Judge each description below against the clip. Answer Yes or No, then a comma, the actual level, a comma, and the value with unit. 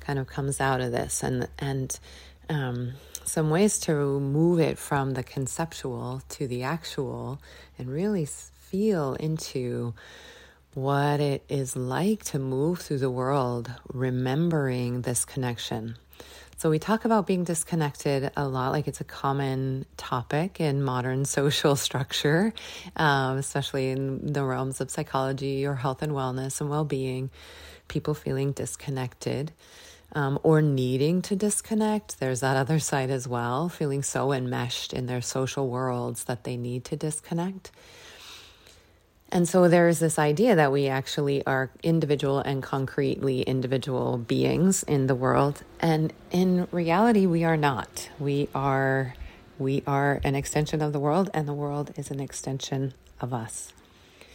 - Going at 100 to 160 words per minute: Yes, average, 145 wpm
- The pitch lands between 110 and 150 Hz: Yes, medium, 140 Hz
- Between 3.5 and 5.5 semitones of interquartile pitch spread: No, average, 3.1 semitones